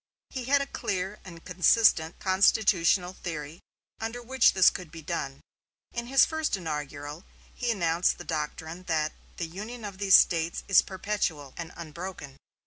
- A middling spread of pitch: Yes, average, 4.5 semitones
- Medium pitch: Yes, medium, 180 Hz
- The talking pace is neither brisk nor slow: Yes, average, 150 wpm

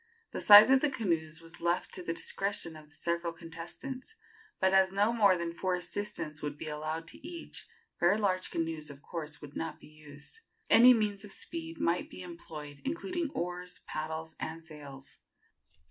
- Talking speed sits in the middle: Yes, average, 175 wpm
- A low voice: No, medium, 170 Hz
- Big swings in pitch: No, average, 4.2 semitones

